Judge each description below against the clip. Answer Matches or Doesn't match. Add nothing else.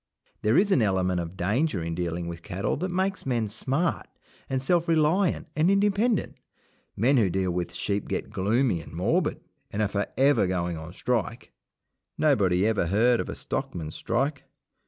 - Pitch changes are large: Matches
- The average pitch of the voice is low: Matches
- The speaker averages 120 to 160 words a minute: Doesn't match